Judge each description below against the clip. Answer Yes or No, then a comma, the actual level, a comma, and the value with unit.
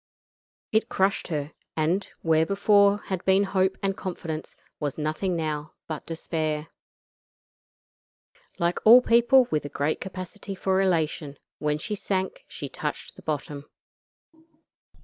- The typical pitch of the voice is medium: Yes, medium, 175 Hz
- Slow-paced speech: Yes, slow, 130 wpm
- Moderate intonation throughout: Yes, average, 4.1 semitones